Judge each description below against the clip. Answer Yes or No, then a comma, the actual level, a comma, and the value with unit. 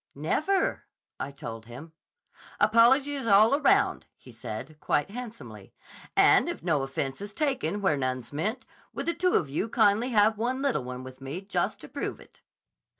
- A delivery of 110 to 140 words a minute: No, average, 165 wpm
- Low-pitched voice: No, high, 200 Hz